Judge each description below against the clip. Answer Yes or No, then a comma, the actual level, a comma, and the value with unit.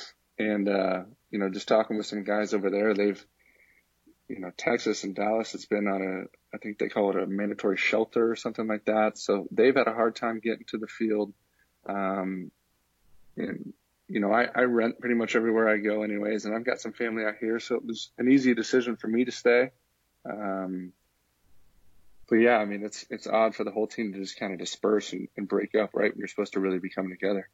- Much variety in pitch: No, average, 2.8 semitones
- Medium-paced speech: No, fast, 220 wpm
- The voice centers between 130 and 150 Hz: No, low, 105 Hz